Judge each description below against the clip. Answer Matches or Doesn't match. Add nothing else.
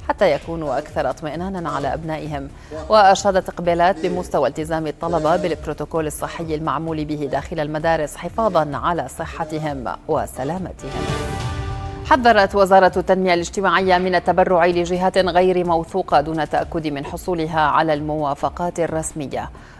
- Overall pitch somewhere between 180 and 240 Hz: Doesn't match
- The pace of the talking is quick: Doesn't match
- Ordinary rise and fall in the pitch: Matches